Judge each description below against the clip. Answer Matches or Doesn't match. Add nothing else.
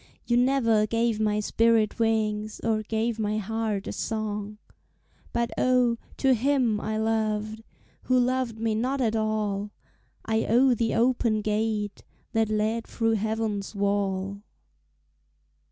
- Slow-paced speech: Matches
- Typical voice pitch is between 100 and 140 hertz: Doesn't match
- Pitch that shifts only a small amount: Matches